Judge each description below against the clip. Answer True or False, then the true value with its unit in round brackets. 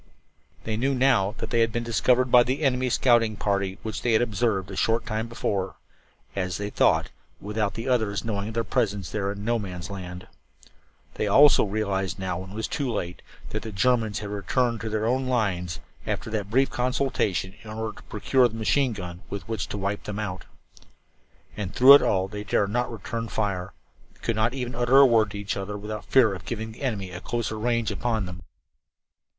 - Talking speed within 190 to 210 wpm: True (205 wpm)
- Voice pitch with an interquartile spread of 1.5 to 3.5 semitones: True (3.2 semitones)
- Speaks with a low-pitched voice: True (110 Hz)